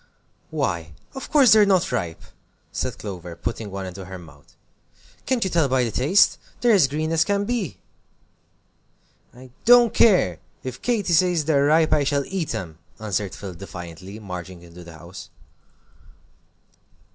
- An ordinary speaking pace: Yes, average, 155 wpm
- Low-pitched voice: Yes, low, 130 Hz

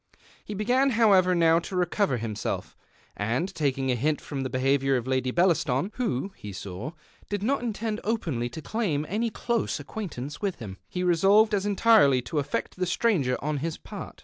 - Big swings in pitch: Yes, wide, 7.8 semitones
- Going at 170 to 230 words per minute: Yes, average, 180 wpm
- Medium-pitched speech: Yes, medium, 165 Hz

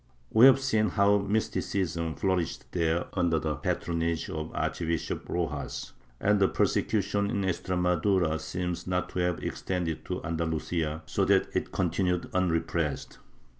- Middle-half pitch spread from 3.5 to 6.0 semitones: No, average, 3.0 semitones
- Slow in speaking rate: Yes, slow, 130 wpm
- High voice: No, very low, 90 Hz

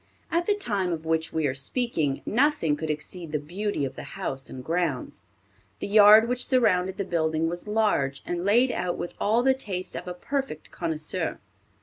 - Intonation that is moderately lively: No, wide, 5.7 semitones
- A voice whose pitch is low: No, medium, 180 Hz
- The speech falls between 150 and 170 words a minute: No, average, 190 wpm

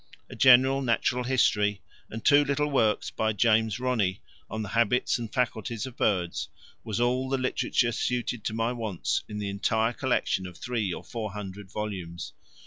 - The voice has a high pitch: No, low, 115 Hz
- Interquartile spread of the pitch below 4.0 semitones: Yes, average, 3.3 semitones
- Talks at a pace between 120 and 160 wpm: No, average, 170 wpm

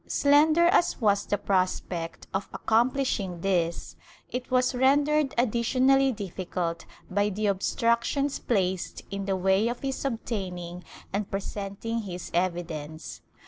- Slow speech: Yes, slow, 120 wpm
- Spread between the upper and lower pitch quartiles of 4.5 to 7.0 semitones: Yes, wide, 5.5 semitones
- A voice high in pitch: Yes, high, 205 Hz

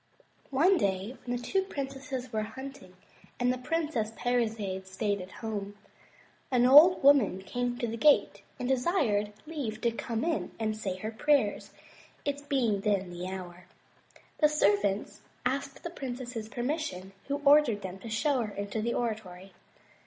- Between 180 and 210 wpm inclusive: No, average, 155 wpm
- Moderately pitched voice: No, high, 235 Hz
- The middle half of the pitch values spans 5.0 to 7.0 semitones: Yes, average, 5.3 semitones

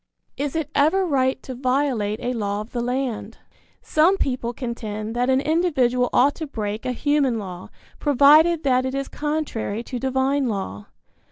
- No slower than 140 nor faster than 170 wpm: Yes, average, 165 wpm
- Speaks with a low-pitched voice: No, very high, 260 Hz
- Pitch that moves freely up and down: No, average, 3.7 semitones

